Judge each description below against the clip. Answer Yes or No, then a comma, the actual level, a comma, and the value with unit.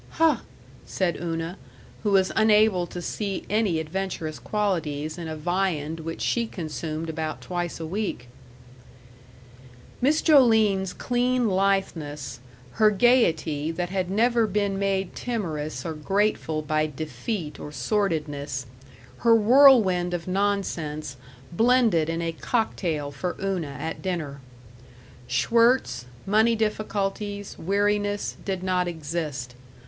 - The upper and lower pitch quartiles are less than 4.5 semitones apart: No, average, 4.9 semitones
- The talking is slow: Yes, slow, 115 wpm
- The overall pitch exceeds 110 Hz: Yes, medium, 185 Hz